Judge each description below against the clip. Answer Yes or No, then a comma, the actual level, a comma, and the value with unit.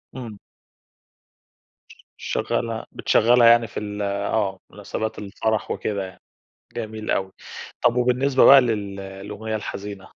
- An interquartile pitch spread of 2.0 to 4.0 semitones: Yes, average, 2.8 semitones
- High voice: No, low, 110 Hz